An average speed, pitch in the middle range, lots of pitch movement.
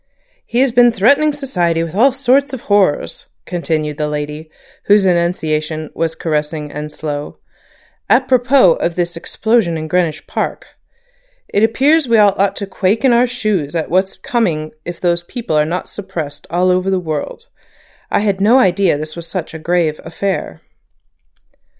Yes: average, 160 wpm; medium, 180 Hz; wide, 6.1 semitones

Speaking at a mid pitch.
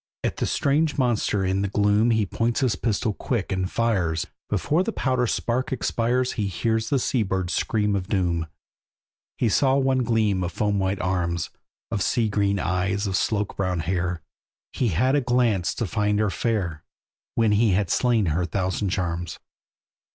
No: low, 105 Hz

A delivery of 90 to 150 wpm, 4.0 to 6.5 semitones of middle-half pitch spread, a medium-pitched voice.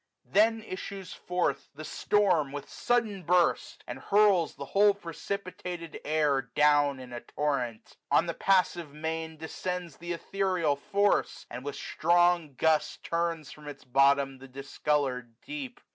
Yes: average, 145 wpm; average, 4.6 semitones; medium, 160 Hz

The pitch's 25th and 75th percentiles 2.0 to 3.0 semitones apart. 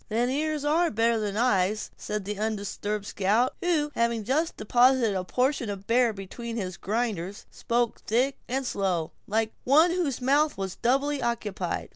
No: average, 4.6 semitones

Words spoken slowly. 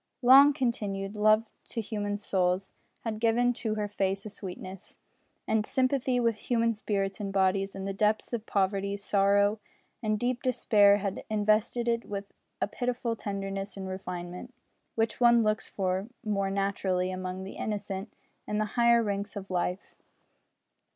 No: average, 150 wpm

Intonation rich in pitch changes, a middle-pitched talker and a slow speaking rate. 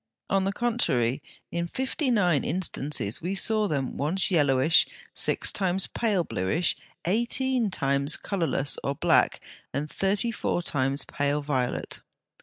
Yes: wide, 6.3 semitones; medium, 170 Hz; slow, 130 wpm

